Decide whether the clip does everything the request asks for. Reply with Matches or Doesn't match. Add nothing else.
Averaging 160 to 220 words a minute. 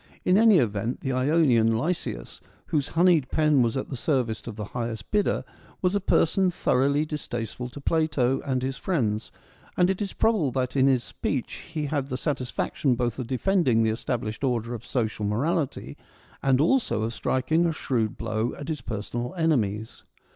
Matches